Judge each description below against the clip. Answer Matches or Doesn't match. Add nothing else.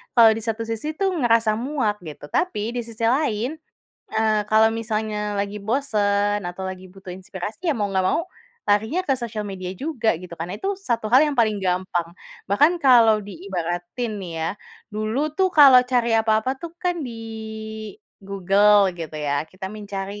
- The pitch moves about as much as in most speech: Matches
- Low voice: Doesn't match